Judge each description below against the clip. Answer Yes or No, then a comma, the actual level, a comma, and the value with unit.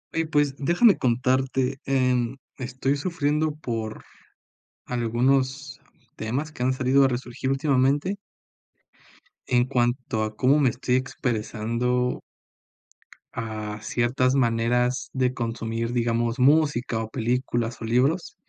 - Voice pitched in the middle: No, low, 125 Hz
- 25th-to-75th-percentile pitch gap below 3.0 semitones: Yes, narrow, 2.5 semitones